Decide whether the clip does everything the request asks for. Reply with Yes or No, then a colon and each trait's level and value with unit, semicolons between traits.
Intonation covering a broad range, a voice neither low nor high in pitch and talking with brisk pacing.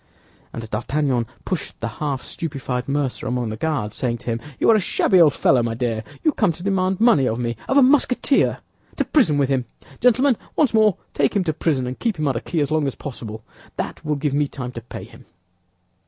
Yes: wide, 7.1 semitones; medium, 145 Hz; fast, 215 wpm